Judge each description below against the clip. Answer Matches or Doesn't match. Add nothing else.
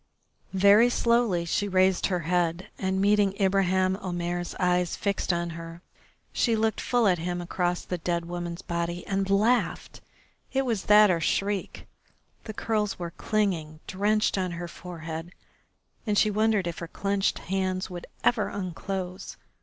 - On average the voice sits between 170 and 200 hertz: Matches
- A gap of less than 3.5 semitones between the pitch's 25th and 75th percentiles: Matches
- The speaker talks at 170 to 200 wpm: Doesn't match